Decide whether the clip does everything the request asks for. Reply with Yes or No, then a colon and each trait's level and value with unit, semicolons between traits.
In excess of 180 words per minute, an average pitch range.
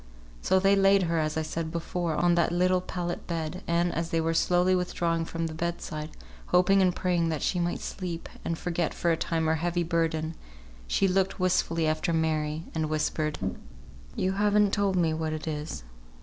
No: average, 190 wpm; narrow, 2.1 semitones